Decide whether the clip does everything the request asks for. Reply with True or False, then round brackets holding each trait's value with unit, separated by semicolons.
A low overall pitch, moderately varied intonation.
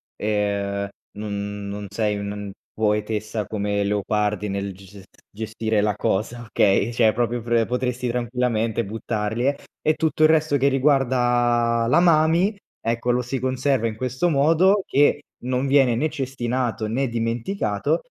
True (115 Hz; 3.8 semitones)